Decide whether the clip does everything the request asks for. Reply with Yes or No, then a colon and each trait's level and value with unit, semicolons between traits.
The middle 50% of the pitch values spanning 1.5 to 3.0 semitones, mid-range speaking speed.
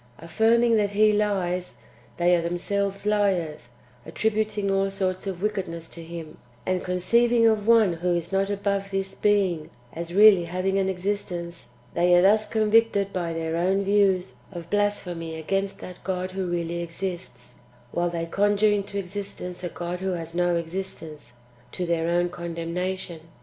Yes: average, 2.7 semitones; average, 160 wpm